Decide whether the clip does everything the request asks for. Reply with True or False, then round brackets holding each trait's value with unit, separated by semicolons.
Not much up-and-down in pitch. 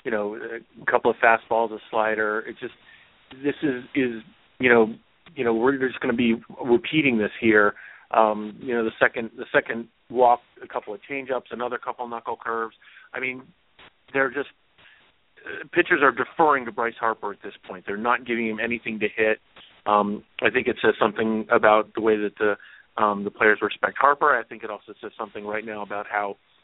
True (2.2 semitones)